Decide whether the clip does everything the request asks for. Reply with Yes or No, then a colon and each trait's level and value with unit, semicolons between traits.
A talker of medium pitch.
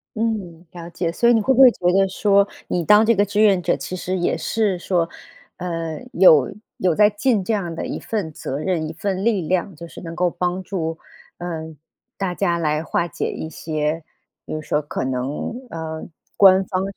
Yes: medium, 180 Hz